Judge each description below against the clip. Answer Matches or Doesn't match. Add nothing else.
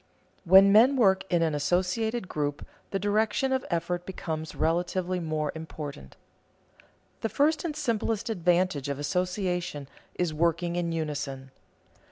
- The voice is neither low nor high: Matches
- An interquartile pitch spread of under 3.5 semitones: Doesn't match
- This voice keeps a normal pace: Doesn't match